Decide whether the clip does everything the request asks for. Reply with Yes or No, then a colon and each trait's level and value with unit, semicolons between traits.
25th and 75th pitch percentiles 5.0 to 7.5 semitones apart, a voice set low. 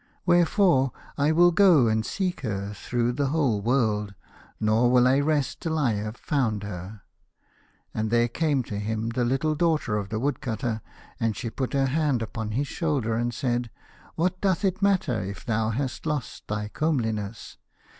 Yes: wide, 5.6 semitones; low, 125 Hz